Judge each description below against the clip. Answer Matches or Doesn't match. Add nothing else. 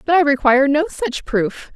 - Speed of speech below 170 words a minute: Doesn't match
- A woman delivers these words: Matches